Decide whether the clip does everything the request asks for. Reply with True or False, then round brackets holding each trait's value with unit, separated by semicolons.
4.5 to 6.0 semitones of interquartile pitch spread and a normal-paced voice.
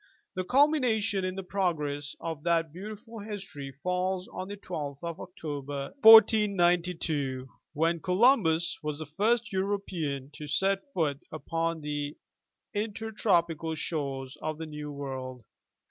False (5.1 semitones; 130 wpm)